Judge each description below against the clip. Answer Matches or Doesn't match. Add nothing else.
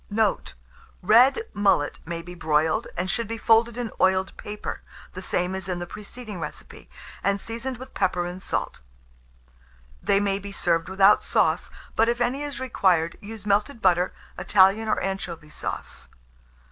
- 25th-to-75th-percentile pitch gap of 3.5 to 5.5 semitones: Matches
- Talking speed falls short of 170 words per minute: Matches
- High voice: Matches